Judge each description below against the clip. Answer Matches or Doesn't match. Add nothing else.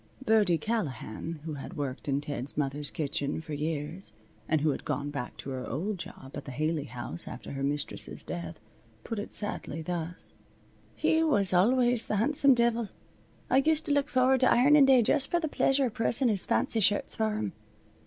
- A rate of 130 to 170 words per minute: Doesn't match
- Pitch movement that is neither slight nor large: Doesn't match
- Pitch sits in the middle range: Matches